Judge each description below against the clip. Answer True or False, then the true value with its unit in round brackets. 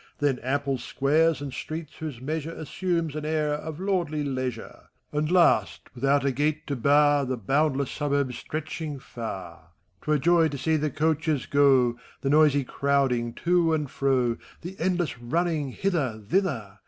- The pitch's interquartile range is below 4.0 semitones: True (3.1 semitones)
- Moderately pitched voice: True (145 Hz)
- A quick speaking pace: False (155 wpm)